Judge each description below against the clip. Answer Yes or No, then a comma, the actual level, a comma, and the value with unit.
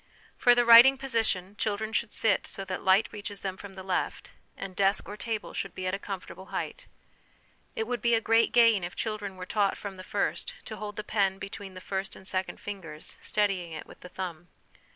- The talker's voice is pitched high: Yes, high, 200 Hz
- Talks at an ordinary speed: No, fast, 215 wpm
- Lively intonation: No, average, 2.8 semitones